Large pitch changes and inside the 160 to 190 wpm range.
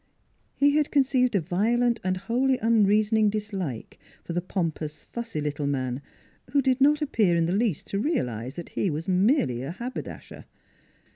Yes: wide, 7.0 semitones; average, 165 wpm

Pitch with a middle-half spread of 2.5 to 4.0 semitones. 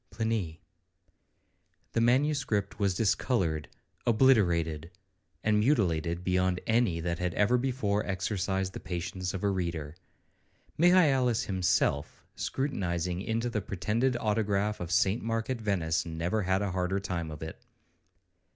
No: average, 4.4 semitones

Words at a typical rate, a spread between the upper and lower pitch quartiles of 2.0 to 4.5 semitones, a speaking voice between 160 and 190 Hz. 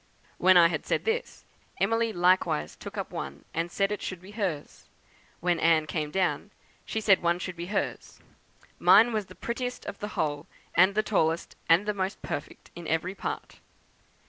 Yes: average, 180 wpm; average, 3.8 semitones; medium, 185 Hz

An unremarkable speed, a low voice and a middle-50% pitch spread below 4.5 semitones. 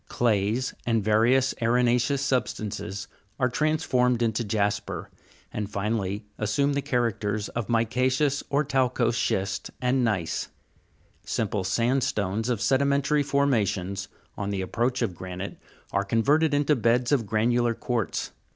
No: slow, 125 wpm; low, 115 Hz; average, 4.0 semitones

